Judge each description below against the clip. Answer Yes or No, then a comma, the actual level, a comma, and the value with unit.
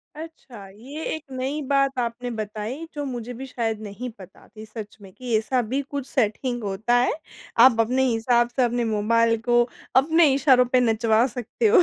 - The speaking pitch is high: Yes, high, 240 Hz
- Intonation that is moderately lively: Yes, average, 3.1 semitones